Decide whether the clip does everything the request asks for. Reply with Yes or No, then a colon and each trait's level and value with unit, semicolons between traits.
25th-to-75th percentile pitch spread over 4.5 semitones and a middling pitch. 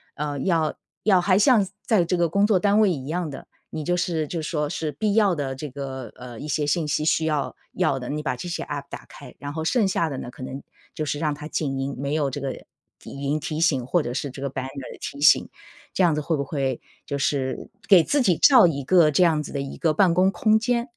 No: average, 4.1 semitones; medium, 150 Hz